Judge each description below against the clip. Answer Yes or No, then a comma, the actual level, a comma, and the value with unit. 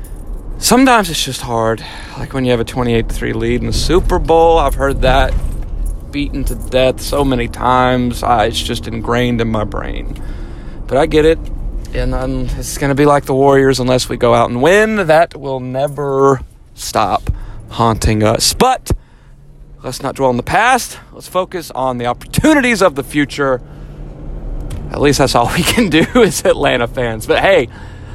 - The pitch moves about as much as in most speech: Yes, average, 3.2 semitones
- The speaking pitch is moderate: No, low, 130 Hz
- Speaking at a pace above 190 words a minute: No, average, 175 wpm